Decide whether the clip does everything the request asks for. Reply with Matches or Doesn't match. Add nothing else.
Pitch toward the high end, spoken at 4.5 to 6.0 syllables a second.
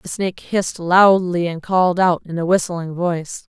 Doesn't match